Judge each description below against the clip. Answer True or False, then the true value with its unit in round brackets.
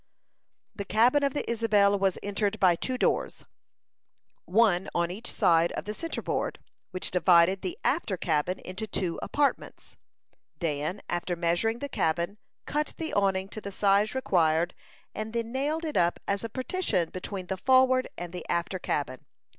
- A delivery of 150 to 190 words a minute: True (160 wpm)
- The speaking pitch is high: True (200 Hz)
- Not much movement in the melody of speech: False (5.0 semitones)